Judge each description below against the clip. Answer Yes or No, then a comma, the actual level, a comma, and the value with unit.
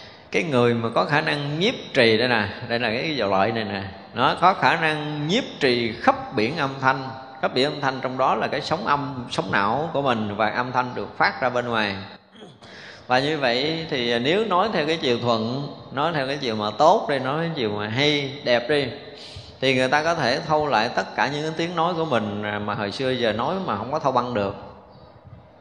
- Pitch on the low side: Yes, low, 130 Hz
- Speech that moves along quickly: No, average, 230 wpm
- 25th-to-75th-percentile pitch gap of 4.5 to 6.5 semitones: Yes, average, 4.9 semitones